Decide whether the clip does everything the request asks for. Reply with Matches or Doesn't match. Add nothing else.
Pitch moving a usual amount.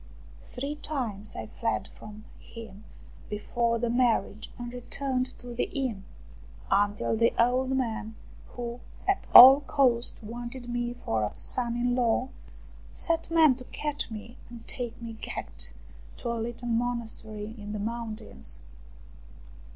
Doesn't match